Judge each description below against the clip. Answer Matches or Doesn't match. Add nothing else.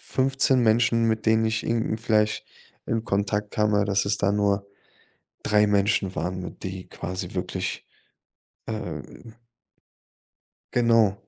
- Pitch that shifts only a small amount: Matches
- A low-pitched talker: Matches